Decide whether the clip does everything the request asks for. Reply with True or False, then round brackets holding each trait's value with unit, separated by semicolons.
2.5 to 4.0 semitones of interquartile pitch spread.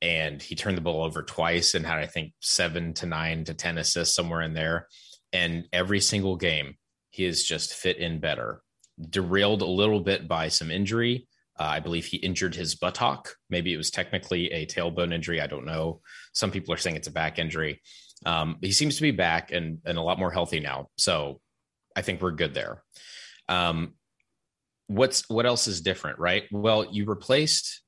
True (3.3 semitones)